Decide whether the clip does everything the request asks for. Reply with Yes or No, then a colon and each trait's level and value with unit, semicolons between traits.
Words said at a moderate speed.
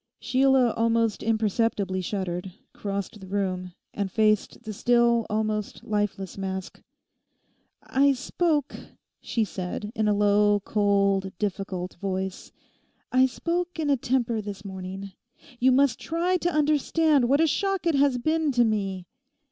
No: slow, 130 wpm